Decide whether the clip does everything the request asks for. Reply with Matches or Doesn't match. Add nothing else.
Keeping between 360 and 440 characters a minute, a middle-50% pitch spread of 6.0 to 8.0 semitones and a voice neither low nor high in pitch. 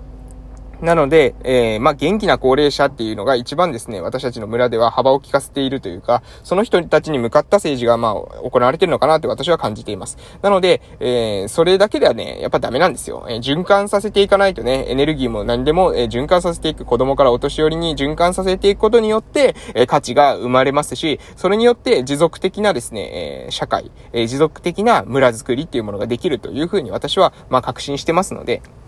Matches